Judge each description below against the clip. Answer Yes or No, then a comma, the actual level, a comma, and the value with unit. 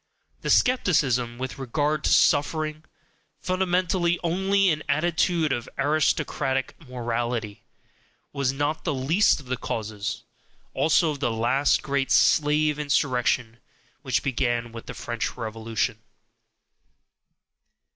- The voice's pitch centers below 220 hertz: Yes, medium, 140 Hz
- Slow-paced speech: Yes, slow, 110 wpm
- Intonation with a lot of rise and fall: No, average, 4.5 semitones